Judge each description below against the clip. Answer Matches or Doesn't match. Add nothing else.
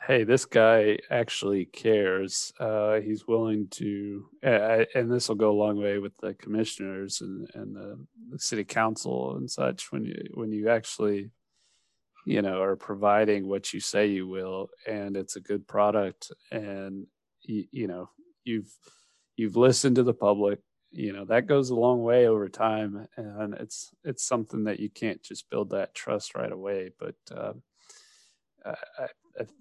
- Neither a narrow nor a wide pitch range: Doesn't match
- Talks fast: Doesn't match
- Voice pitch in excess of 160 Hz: Doesn't match